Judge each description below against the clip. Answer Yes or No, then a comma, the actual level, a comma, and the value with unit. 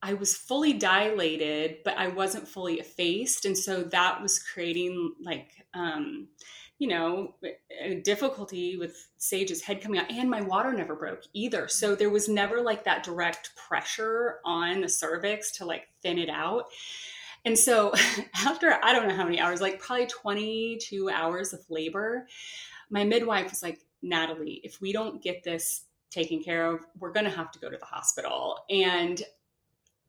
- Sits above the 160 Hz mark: Yes, high, 190 Hz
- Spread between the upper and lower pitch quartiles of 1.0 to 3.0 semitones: No, average, 3.8 semitones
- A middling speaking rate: Yes, average, 170 wpm